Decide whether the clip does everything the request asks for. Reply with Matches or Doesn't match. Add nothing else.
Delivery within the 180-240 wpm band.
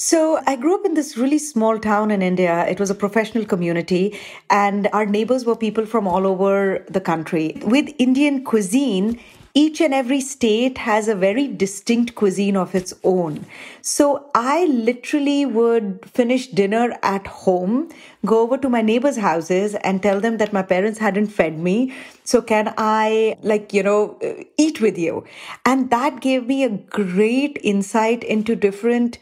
Doesn't match